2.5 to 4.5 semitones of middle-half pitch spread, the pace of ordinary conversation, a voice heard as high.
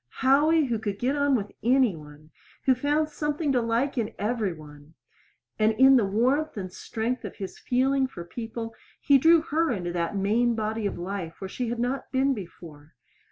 No: wide, 5.6 semitones; average, 190 wpm; high, 230 Hz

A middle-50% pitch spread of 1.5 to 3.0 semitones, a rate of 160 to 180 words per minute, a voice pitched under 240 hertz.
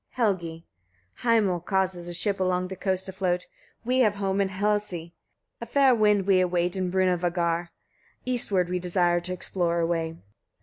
Yes: narrow, 2.4 semitones; average, 170 wpm; medium, 185 Hz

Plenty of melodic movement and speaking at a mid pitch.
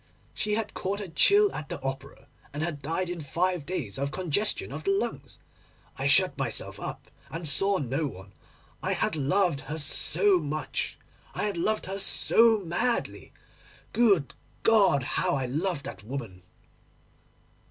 Yes: wide, 6.0 semitones; medium, 165 Hz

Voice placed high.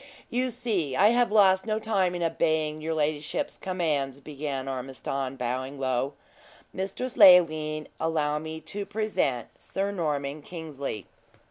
No: medium, 155 Hz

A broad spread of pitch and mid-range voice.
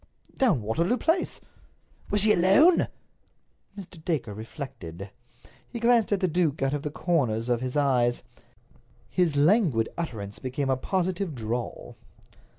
Yes: wide, 7.5 semitones; medium, 150 Hz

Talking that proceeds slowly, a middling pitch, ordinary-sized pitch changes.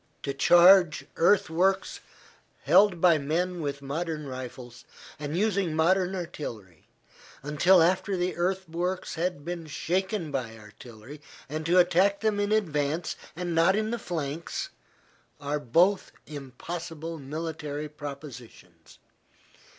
Yes: slow, 115 wpm; medium, 165 Hz; average, 4.1 semitones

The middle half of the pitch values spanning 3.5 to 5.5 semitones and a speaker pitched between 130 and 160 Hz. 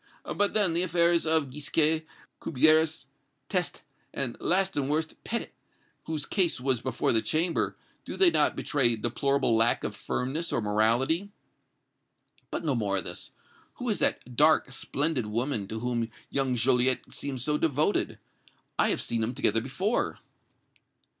Yes: average, 5.2 semitones; medium, 140 Hz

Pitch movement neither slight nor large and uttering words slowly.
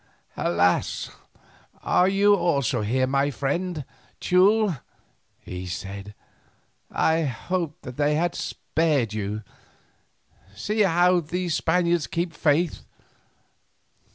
No: wide, 5.9 semitones; slow, 100 wpm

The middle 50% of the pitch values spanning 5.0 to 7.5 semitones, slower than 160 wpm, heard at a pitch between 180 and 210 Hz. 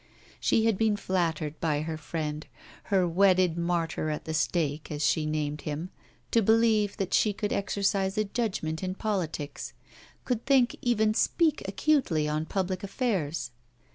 Yes: average, 5.3 semitones; average, 150 wpm; medium, 185 Hz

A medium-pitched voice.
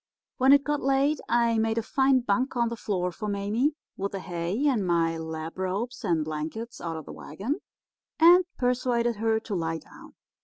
No: high, 220 Hz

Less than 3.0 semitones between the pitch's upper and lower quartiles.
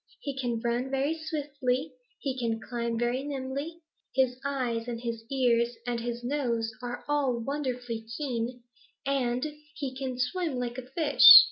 Yes: narrow, 2.5 semitones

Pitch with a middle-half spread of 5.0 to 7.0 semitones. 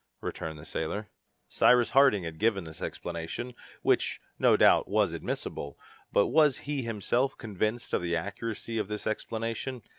Yes: wide, 5.6 semitones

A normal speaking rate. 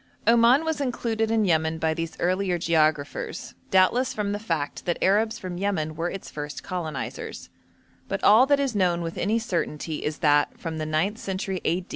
Yes: average, 180 wpm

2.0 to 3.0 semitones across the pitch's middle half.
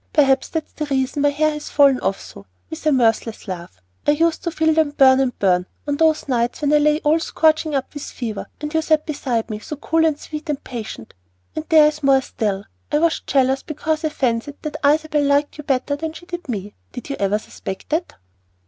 No: average, 3.5 semitones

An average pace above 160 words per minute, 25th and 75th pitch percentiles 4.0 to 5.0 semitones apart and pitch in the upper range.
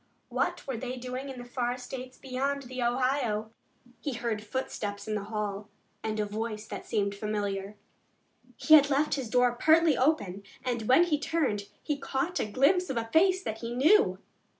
Yes: average, 180 wpm; average, 4.5 semitones; high, 245 Hz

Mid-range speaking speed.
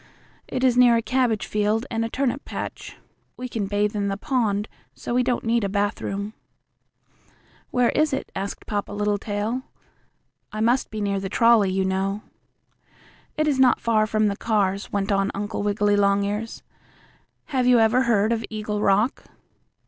Yes: average, 165 wpm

